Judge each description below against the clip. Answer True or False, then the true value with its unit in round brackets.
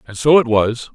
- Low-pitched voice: True (125 Hz)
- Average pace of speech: False (255 wpm)